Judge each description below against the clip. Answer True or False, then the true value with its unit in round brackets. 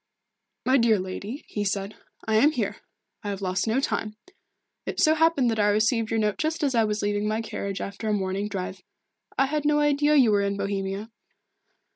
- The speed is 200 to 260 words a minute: True (205 wpm)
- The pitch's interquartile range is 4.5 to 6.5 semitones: True (4.9 semitones)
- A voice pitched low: False (215 Hz)